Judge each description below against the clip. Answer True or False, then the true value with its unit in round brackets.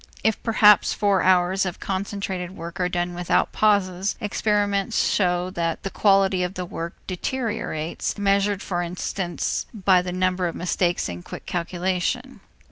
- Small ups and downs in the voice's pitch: True (2.2 semitones)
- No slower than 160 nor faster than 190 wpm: False (145 wpm)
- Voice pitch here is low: False (185 Hz)